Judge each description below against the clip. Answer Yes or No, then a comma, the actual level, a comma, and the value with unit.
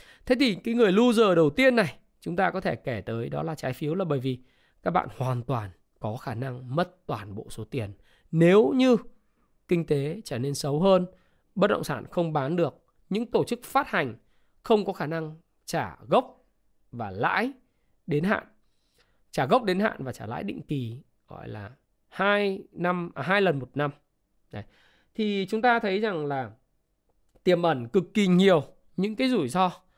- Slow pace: No, average, 190 wpm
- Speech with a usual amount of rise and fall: No, wide, 7.3 semitones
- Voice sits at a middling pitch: Yes, medium, 165 Hz